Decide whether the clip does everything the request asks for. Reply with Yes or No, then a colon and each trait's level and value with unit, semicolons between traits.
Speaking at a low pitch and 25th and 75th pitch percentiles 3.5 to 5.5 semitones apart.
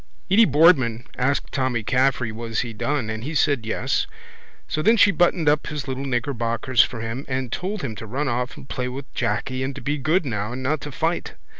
Yes: low, 130 Hz; average, 4.0 semitones